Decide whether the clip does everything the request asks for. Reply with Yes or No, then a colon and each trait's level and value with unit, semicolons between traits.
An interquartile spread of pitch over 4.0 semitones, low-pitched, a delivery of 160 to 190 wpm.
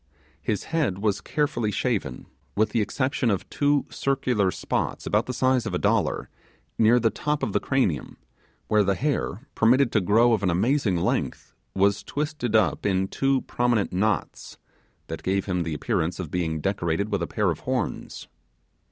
Yes: average, 5.3 semitones; low, 110 Hz; average, 170 wpm